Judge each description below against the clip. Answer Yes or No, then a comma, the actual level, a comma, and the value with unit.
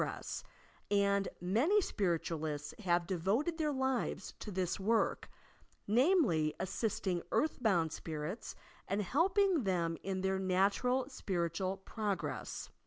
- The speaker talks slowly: Yes, slow, 110 wpm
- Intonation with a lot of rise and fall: Yes, wide, 6.0 semitones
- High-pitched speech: Yes, high, 195 Hz